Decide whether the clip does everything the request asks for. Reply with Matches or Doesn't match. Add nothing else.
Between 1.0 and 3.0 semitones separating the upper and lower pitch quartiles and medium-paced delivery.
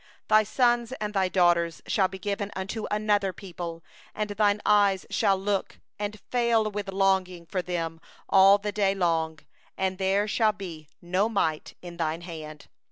Matches